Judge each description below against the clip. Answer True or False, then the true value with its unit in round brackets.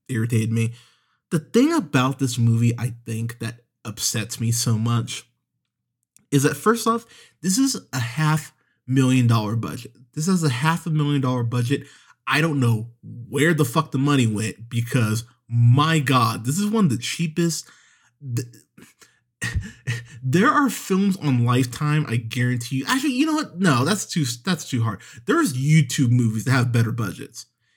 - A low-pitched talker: True (130 Hz)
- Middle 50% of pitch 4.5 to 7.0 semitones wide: True (4.9 semitones)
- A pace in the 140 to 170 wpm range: True (165 wpm)